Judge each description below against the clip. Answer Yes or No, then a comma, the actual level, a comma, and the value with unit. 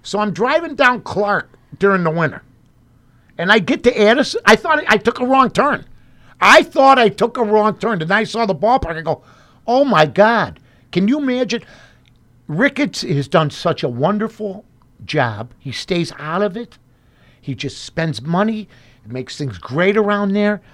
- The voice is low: No, high, 195 Hz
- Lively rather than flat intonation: Yes, wide, 8.6 semitones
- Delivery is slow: No, average, 180 wpm